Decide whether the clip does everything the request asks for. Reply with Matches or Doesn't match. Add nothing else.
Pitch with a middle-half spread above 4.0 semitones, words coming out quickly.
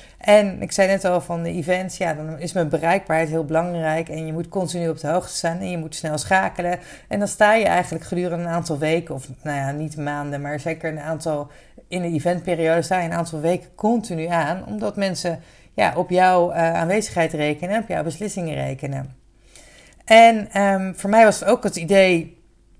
Doesn't match